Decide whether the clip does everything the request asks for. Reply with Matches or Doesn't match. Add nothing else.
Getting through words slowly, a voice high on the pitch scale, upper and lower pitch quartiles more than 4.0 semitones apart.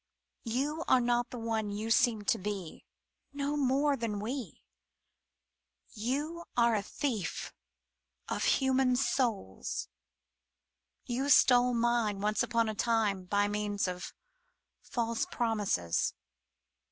Doesn't match